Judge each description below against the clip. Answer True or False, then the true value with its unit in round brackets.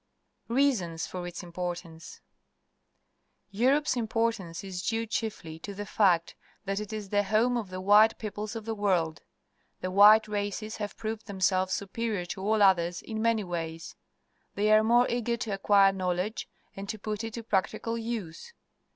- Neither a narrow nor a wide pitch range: True (3.3 semitones)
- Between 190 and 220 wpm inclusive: False (170 wpm)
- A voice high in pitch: True (205 Hz)